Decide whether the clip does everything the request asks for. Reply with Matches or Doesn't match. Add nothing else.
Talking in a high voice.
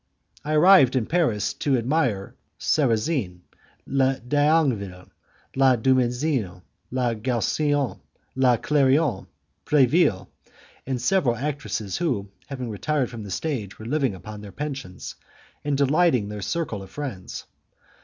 Doesn't match